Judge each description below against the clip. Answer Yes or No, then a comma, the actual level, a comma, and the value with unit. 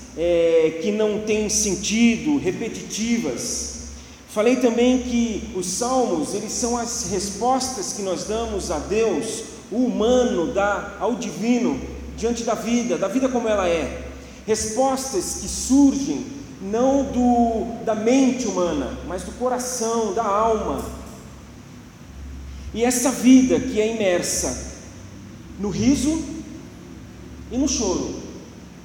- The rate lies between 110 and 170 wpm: Yes, slow, 120 wpm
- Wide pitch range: No, average, 3.7 semitones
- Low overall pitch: No, high, 230 Hz